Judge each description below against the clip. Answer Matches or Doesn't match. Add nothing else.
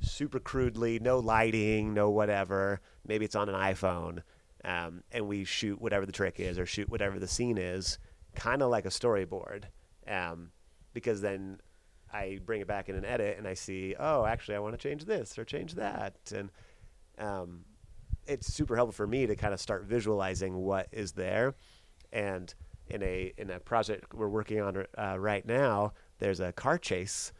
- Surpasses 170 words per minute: Matches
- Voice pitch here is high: Doesn't match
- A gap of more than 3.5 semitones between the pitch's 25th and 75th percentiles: Doesn't match